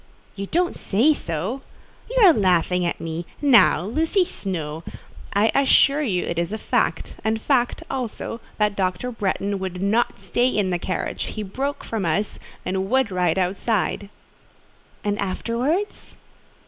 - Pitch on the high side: Yes, high, 205 Hz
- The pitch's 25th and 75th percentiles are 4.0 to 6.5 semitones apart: Yes, wide, 5.4 semitones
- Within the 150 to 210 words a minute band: No, average, 140 wpm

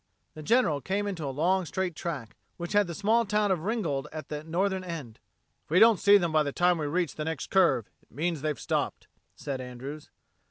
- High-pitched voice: No, medium, 170 Hz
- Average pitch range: Yes, average, 4.3 semitones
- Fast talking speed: Yes, fast, 215 wpm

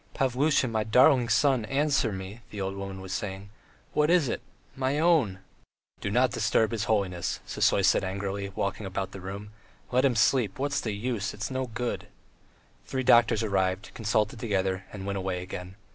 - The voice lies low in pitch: Yes, low, 105 Hz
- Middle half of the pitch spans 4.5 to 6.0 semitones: Yes, average, 4.8 semitones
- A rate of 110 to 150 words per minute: No, average, 175 wpm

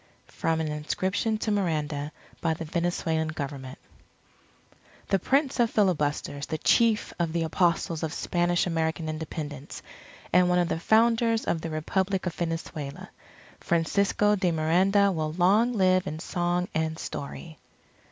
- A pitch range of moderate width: Yes, average, 3.3 semitones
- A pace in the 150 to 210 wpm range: No, average, 140 wpm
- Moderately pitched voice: Yes, medium, 170 Hz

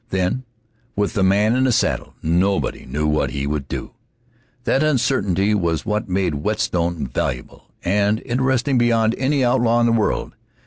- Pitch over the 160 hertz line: No, low, 105 Hz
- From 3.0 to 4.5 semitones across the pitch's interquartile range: No, wide, 5.4 semitones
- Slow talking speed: No, average, 155 wpm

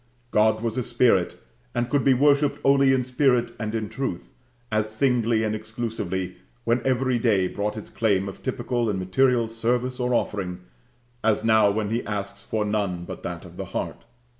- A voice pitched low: Yes, low, 115 Hz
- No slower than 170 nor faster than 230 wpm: Yes, average, 180 wpm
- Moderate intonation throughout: Yes, average, 3.1 semitones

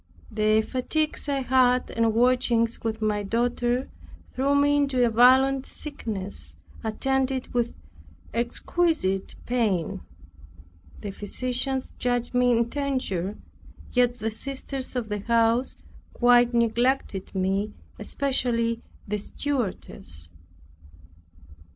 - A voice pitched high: Yes, high, 240 Hz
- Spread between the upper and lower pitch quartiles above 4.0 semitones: No, average, 3.1 semitones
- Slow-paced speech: Yes, slow, 100 wpm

